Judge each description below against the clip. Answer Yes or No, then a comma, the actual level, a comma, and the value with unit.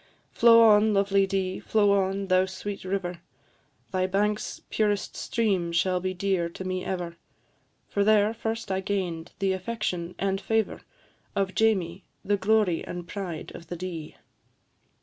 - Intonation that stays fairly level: Yes, narrow, 2.1 semitones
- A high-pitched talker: Yes, high, 195 Hz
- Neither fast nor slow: Yes, average, 150 wpm